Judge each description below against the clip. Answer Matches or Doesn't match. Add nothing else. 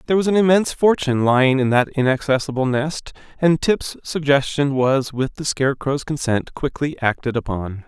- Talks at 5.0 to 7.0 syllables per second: Matches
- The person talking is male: Matches